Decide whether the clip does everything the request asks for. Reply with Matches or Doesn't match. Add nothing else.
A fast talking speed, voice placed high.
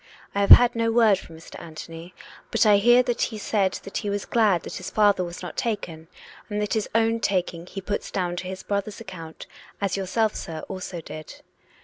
Matches